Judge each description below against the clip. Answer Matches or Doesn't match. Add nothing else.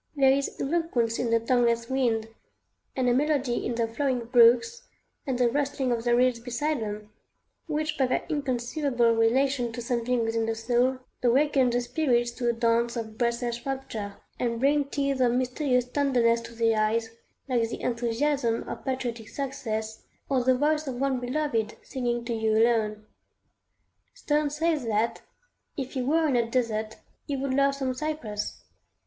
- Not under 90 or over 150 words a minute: Doesn't match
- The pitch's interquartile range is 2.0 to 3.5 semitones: Matches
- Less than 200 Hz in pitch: Doesn't match